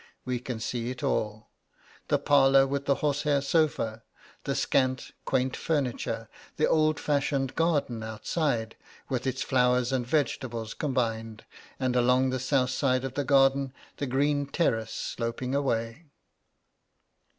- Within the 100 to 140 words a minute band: Yes, slow, 135 wpm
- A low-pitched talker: Yes, low, 130 Hz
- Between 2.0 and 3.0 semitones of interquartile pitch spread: Yes, average, 2.7 semitones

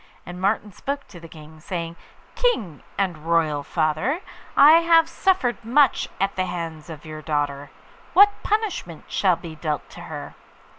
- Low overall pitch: No, medium, 175 Hz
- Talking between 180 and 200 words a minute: No, average, 155 wpm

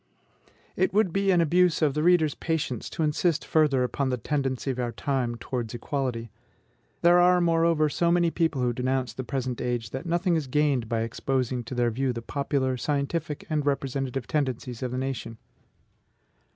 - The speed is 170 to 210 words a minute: Yes, average, 180 wpm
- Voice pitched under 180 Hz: Yes, low, 135 Hz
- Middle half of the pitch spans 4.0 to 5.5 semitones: Yes, average, 4.4 semitones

